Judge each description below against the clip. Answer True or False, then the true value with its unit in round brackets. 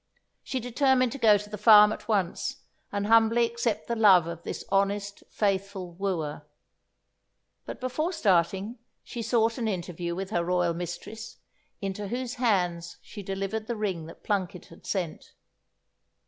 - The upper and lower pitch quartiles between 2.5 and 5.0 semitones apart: True (4.0 semitones)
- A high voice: True (205 Hz)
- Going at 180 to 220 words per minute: False (150 wpm)